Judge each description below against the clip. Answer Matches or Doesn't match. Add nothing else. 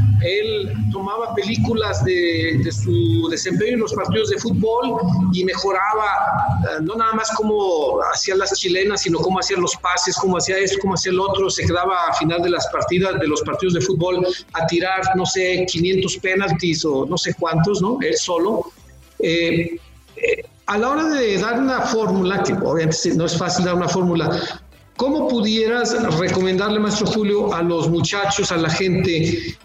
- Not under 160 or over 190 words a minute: Matches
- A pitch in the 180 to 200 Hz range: Matches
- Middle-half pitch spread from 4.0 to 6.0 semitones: Doesn't match